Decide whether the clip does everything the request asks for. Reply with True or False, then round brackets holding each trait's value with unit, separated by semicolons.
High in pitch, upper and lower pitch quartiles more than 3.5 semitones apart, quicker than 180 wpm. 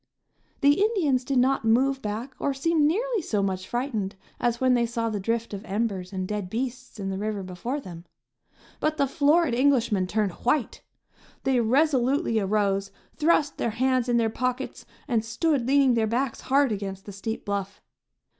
False (235 Hz; 4.7 semitones; 175 wpm)